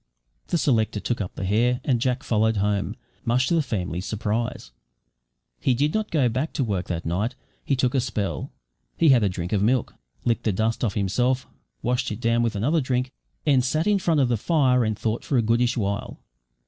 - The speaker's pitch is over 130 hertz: No, low, 120 Hz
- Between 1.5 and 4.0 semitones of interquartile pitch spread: Yes, average, 3.7 semitones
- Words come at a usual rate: No, fast, 210 wpm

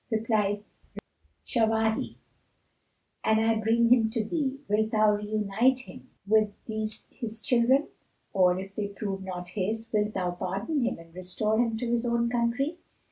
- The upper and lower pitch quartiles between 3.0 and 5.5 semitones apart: No, narrow, 2.5 semitones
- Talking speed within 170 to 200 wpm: No, average, 150 wpm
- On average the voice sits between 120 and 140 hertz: No, high, 220 Hz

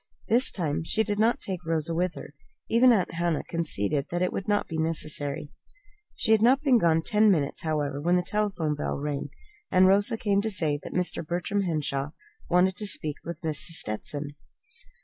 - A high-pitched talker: No, medium, 170 Hz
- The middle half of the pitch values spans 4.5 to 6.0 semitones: Yes, average, 5.0 semitones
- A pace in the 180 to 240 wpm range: Yes, average, 190 wpm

